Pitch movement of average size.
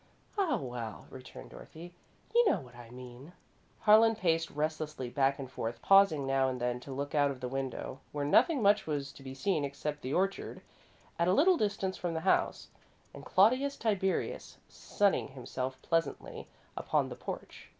No: wide, 6.6 semitones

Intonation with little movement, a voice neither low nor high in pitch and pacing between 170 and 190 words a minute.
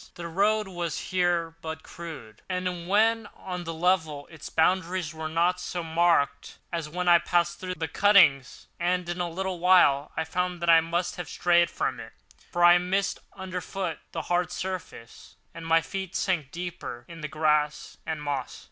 Yes: narrow, 2.1 semitones; medium, 175 Hz; average, 175 wpm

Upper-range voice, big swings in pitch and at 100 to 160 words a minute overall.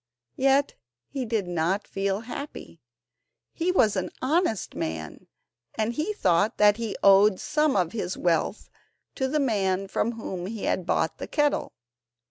Yes: high, 215 Hz; wide, 6.0 semitones; average, 150 wpm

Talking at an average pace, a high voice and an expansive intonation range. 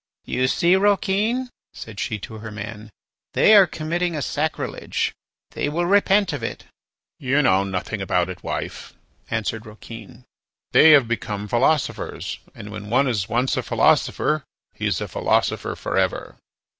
No: average, 155 wpm; low, 125 Hz; wide, 7.9 semitones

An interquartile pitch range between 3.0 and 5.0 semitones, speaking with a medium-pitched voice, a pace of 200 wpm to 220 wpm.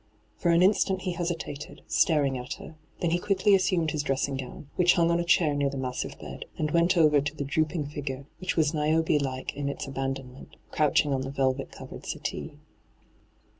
Yes: average, 3.7 semitones; medium, 150 Hz; fast, 205 wpm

